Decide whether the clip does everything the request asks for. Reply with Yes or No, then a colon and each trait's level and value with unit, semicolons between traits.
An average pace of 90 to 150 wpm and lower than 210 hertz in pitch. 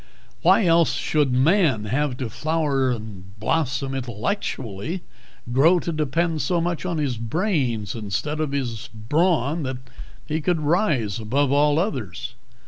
Yes: average, 140 wpm; medium, 140 Hz